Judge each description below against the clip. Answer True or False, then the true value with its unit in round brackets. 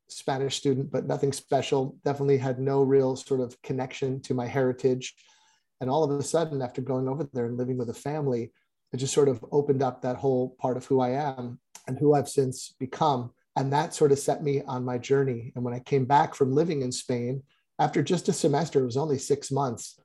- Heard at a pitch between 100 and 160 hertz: True (135 Hz)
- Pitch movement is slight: True (1.8 semitones)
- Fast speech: True (220 wpm)